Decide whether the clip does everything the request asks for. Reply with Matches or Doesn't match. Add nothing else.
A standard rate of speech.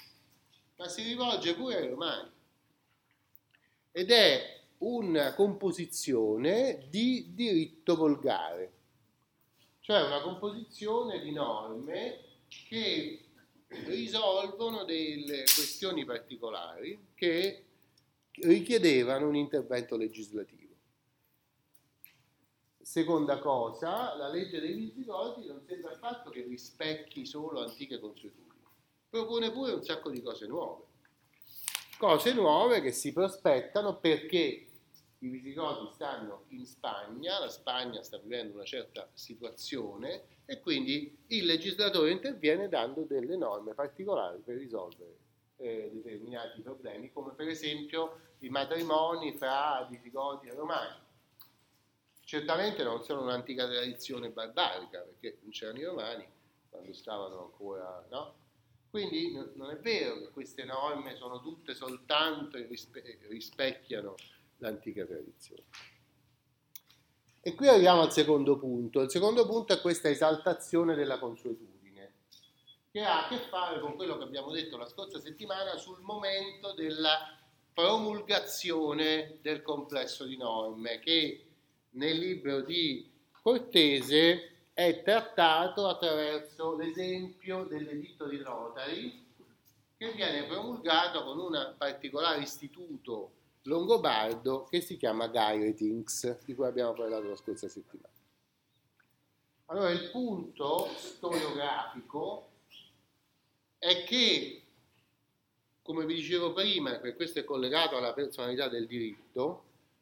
Doesn't match